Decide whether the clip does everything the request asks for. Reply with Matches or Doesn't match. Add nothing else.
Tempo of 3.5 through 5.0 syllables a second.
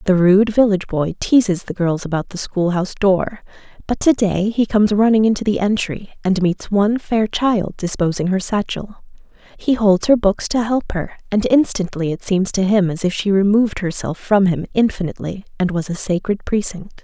Doesn't match